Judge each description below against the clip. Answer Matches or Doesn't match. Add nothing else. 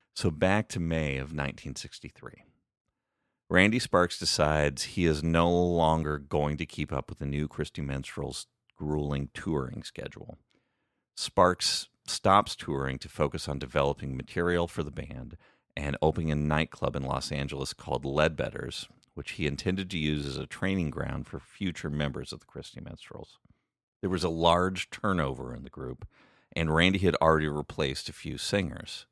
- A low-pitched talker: Matches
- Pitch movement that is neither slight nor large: Matches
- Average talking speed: Matches